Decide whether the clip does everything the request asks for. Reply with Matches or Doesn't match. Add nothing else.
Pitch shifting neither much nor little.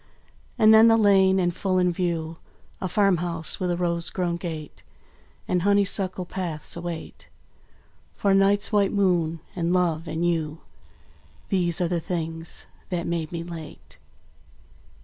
Doesn't match